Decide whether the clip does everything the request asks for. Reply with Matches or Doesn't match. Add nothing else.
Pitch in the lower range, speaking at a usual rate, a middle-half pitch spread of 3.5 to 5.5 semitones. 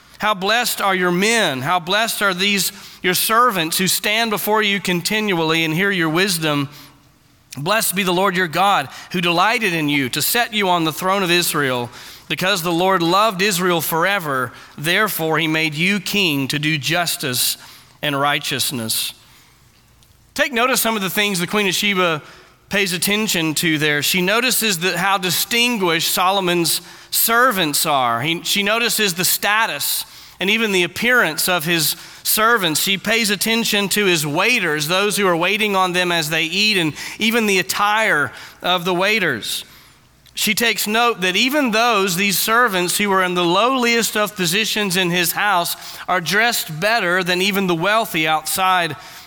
Doesn't match